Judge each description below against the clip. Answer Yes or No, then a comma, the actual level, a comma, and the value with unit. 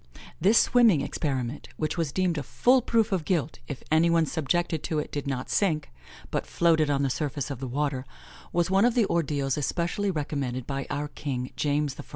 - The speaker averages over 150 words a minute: Yes, average, 195 wpm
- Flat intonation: No, average, 3.9 semitones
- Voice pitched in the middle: Yes, medium, 150 Hz